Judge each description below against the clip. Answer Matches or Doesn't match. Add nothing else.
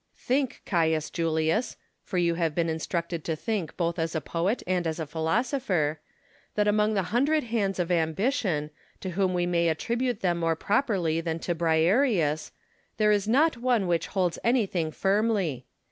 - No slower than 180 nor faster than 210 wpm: Doesn't match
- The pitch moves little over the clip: Doesn't match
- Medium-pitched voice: Matches